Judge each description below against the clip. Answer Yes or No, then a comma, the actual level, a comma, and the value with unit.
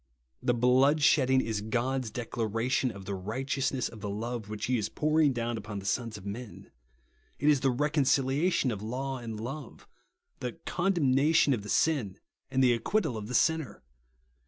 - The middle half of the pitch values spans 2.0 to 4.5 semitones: Yes, average, 3.8 semitones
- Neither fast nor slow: Yes, average, 165 wpm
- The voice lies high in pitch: No, low, 125 Hz